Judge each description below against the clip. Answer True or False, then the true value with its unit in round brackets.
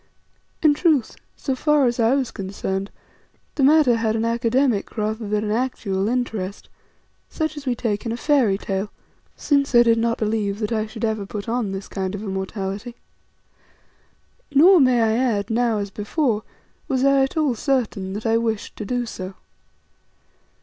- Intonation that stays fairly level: False (3.8 semitones)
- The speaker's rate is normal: True (170 wpm)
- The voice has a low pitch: False (230 Hz)